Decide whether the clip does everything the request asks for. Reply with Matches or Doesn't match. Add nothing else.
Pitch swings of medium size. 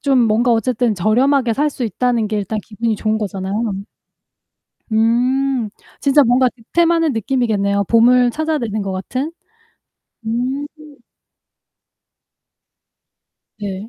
Matches